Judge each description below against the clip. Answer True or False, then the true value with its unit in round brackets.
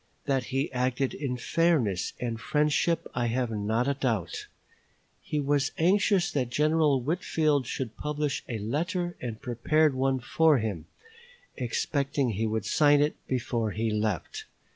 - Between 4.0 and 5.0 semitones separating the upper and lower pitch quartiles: True (4.6 semitones)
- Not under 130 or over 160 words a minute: True (140 wpm)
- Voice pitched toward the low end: True (130 Hz)